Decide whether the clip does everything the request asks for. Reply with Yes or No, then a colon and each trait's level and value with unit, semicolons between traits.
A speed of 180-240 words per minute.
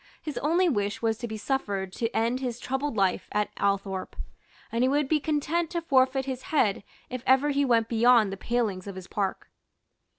Yes: average, 195 wpm